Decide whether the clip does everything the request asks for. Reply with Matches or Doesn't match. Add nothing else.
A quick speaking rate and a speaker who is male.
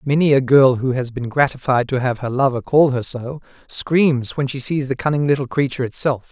Matches